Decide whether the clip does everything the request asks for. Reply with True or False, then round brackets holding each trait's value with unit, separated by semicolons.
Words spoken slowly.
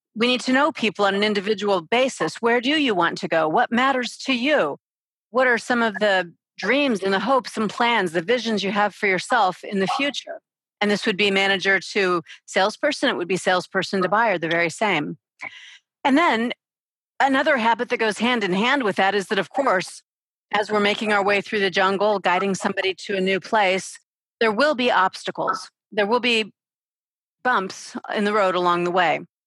False (200 wpm)